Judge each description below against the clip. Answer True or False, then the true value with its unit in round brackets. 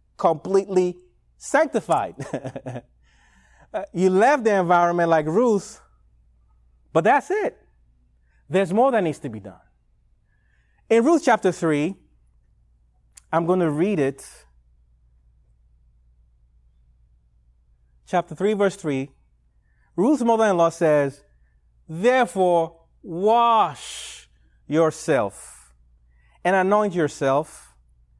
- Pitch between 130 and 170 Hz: True (135 Hz)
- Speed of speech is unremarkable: False (90 wpm)